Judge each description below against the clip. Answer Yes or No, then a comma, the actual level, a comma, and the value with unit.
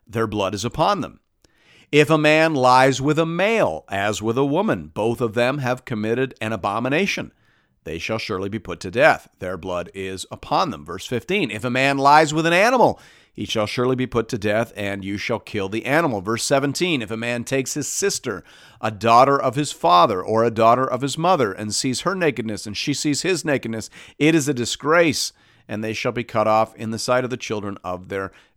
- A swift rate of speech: Yes, fast, 215 wpm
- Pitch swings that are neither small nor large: Yes, average, 4.6 semitones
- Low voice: Yes, low, 115 Hz